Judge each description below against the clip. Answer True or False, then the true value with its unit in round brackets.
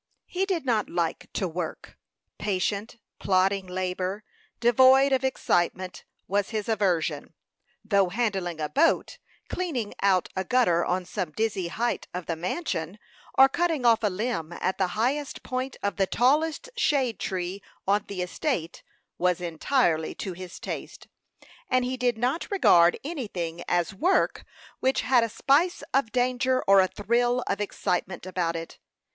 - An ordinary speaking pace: True (150 wpm)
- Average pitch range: False (5.9 semitones)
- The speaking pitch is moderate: False (205 Hz)